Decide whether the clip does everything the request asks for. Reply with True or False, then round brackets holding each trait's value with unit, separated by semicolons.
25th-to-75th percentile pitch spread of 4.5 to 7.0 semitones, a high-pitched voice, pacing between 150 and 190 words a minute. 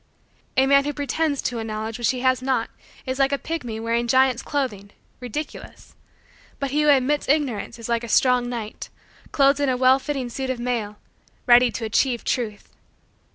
False (2.8 semitones; 255 Hz; 185 wpm)